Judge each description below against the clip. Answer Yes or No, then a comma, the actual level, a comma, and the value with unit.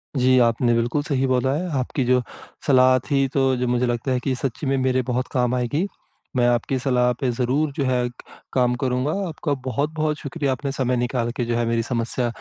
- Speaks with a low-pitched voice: Yes, low, 130 Hz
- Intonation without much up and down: Yes, narrow, 1.9 semitones